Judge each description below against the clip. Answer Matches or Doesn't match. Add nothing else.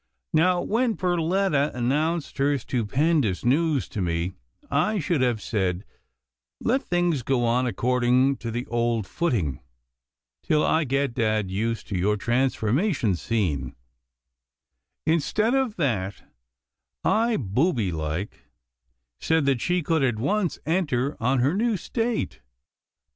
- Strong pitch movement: Matches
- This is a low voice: Matches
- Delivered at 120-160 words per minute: Matches